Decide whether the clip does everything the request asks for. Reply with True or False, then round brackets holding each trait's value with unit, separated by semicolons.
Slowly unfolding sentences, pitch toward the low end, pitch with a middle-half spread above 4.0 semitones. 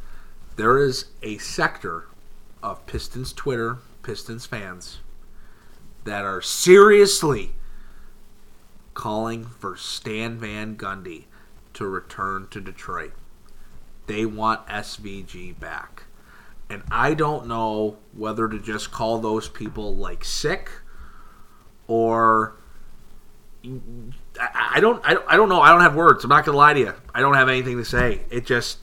False (130 wpm; 110 Hz; 2.6 semitones)